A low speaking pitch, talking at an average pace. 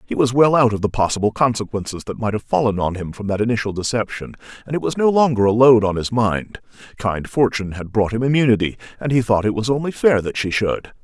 No: low, 115 Hz; fast, 240 wpm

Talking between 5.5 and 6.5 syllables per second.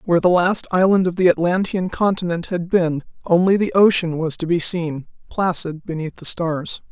No: 5.0 syllables/s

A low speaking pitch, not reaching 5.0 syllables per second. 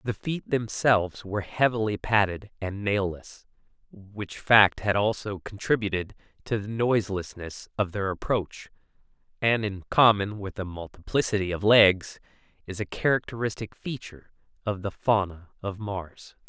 Yes: low, 105 Hz; 4.6 syllables/s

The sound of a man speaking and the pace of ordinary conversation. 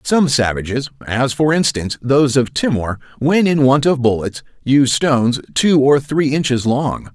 Yes: male; average, 150 wpm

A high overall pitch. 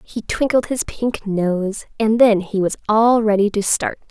Yes: high, 215 Hz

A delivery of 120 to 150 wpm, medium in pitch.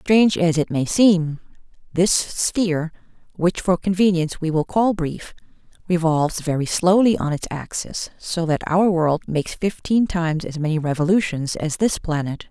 No: average, 160 wpm; medium, 170 Hz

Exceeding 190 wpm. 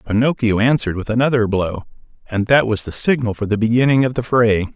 Yes: average, 200 wpm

